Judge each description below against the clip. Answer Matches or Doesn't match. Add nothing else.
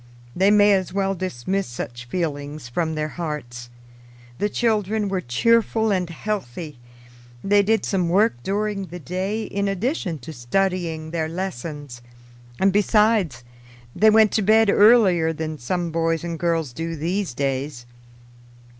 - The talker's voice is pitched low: Doesn't match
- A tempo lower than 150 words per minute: Matches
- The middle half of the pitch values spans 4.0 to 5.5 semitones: Matches